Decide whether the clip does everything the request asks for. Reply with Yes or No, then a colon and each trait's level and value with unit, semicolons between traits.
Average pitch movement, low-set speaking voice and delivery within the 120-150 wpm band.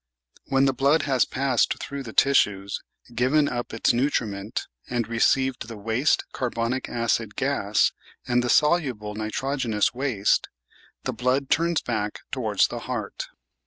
Yes: average, 3.5 semitones; low, 125 Hz; average, 145 wpm